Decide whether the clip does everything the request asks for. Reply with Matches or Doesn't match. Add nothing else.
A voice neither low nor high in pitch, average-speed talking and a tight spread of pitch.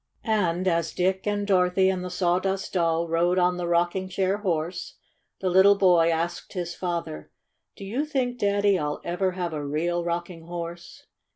Matches